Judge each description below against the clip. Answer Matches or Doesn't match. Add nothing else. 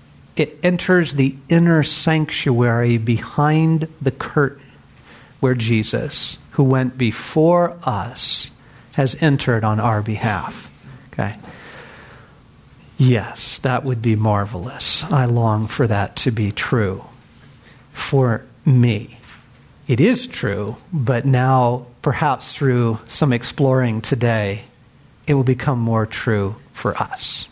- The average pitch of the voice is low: Matches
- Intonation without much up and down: Doesn't match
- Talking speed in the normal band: Doesn't match